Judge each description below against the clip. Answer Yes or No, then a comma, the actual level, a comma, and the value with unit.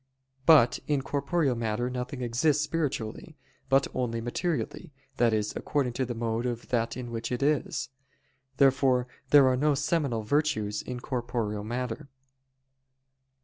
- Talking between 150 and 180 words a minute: No, average, 140 wpm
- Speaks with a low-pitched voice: Yes, low, 125 Hz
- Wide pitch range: No, average, 3.5 semitones